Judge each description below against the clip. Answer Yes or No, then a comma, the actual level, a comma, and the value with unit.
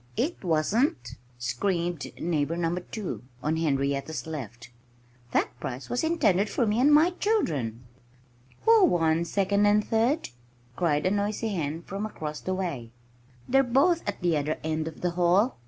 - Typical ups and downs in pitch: No, wide, 5.9 semitones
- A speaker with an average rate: Yes, average, 155 wpm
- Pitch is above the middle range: No, medium, 175 Hz